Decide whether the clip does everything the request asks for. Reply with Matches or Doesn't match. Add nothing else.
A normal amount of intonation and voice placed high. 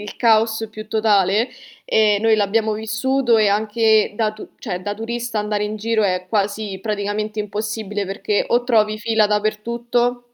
Doesn't match